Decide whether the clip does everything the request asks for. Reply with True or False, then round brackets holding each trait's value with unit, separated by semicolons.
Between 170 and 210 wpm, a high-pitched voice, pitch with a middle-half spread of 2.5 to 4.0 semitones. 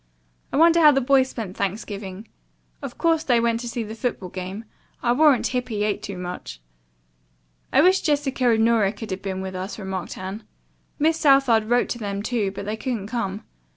False (185 wpm; 225 Hz; 4.6 semitones)